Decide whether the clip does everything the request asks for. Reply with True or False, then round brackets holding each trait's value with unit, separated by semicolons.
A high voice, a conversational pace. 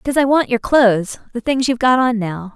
False (240 Hz; 235 wpm)